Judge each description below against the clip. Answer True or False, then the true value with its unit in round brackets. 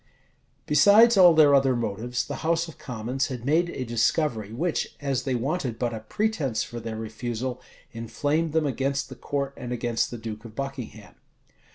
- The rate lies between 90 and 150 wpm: False (175 wpm)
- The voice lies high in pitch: False (130 Hz)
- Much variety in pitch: False (4.4 semitones)